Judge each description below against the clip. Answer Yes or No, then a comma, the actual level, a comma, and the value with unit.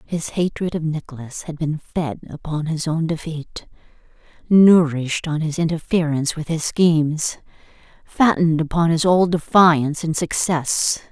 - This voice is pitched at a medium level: Yes, medium, 160 Hz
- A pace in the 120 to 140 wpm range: Yes, slow, 135 wpm